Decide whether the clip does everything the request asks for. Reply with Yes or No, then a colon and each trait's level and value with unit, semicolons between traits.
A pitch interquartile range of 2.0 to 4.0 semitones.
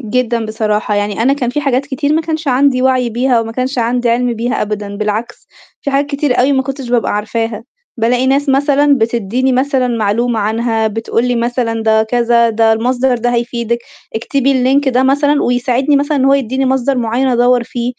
Yes: average, 2.7 semitones